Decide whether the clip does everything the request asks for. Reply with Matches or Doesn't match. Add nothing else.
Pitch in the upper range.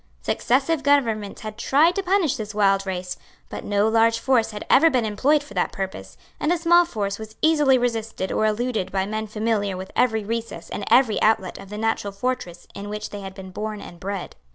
Matches